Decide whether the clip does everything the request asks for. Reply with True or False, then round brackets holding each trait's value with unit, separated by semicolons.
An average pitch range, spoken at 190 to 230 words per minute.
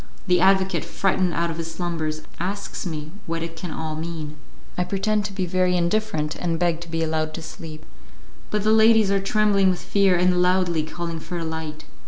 True (3.0 semitones; 200 wpm)